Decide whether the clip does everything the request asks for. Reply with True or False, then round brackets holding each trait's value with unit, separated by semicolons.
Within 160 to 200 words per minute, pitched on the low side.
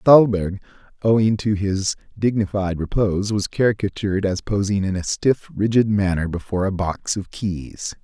False (150 wpm; 100 Hz)